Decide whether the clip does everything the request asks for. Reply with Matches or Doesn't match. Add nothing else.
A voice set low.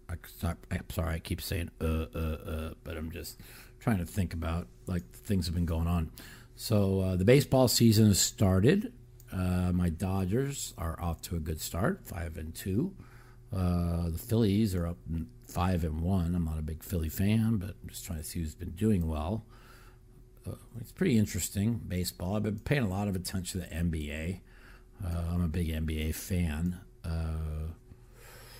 Matches